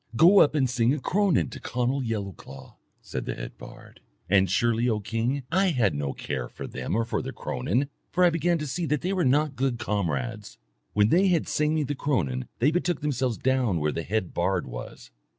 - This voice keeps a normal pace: No, fast, 210 wpm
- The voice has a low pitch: Yes, low, 125 Hz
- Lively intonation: Yes, wide, 7.4 semitones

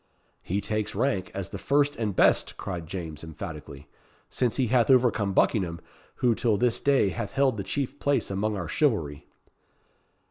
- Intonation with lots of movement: Yes, wide, 5.9 semitones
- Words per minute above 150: Yes, average, 165 wpm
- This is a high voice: No, low, 105 Hz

